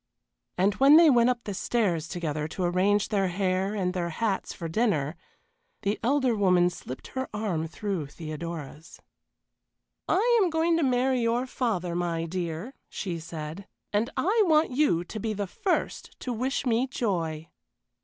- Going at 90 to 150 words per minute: No, average, 160 wpm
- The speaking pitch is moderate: No, high, 200 Hz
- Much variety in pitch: Yes, wide, 6.4 semitones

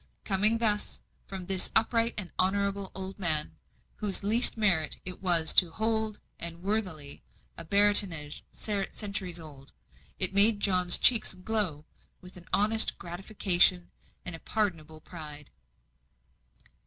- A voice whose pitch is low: No, high, 190 Hz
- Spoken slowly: Yes, slow, 125 wpm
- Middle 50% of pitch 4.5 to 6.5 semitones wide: No, average, 3.5 semitones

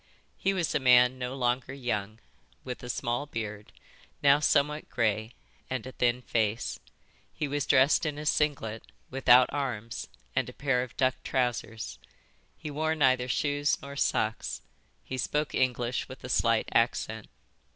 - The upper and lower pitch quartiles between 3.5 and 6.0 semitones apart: No, average, 3.1 semitones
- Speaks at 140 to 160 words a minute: Yes, average, 150 wpm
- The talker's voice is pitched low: Yes, low, 130 Hz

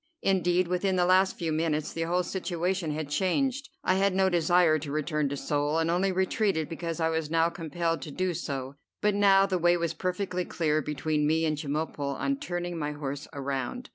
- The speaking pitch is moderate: Yes, medium, 170 Hz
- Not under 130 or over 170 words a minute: No, average, 195 wpm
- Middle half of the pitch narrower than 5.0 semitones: Yes, average, 3.4 semitones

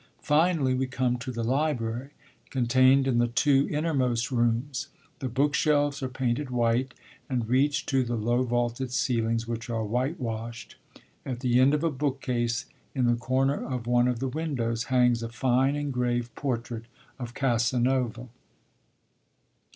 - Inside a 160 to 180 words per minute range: No, average, 150 wpm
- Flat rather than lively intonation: Yes, narrow, 2.2 semitones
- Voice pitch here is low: Yes, low, 125 Hz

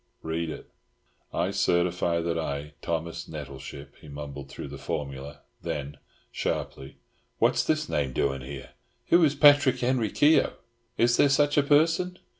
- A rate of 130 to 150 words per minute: Yes, average, 145 wpm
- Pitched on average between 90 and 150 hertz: No, very low, 80 Hz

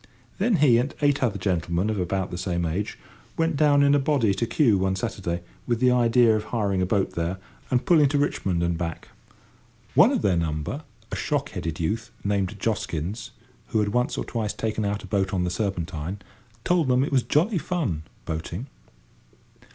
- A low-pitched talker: Yes, low, 105 Hz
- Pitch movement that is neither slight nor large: No, wide, 6.2 semitones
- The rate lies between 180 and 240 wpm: Yes, average, 190 wpm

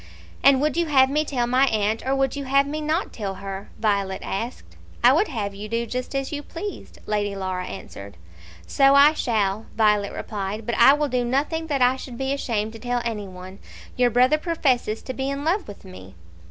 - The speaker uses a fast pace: Yes, fast, 210 wpm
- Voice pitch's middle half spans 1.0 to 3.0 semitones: No, average, 5.1 semitones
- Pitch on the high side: Yes, high, 245 Hz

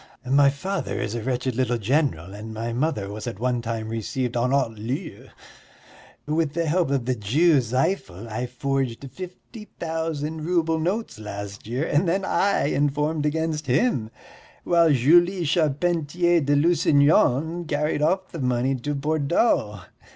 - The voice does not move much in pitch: No, average, 5.2 semitones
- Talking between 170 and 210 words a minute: No, average, 150 wpm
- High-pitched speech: No, medium, 140 Hz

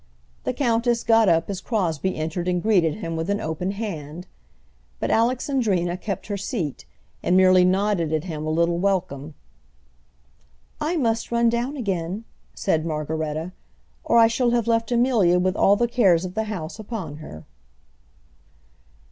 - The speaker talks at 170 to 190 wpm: No, average, 155 wpm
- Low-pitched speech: No, high, 190 Hz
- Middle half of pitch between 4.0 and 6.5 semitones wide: Yes, wide, 5.6 semitones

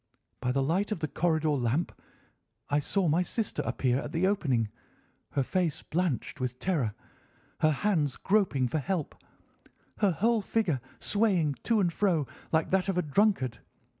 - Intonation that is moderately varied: No, wide, 5.7 semitones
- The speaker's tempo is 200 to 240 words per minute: No, average, 160 wpm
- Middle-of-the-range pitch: Yes, medium, 165 Hz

